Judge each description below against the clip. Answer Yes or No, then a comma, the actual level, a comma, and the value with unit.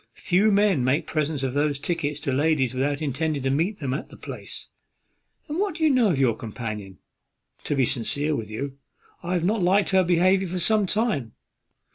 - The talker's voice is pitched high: No, medium, 155 Hz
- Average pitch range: No, wide, 5.9 semitones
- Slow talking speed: No, average, 195 wpm